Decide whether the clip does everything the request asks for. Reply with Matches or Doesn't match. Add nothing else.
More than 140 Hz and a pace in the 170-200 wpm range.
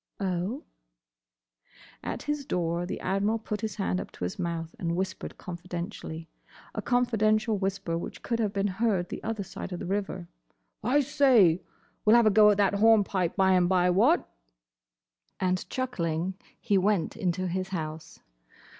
Doesn't match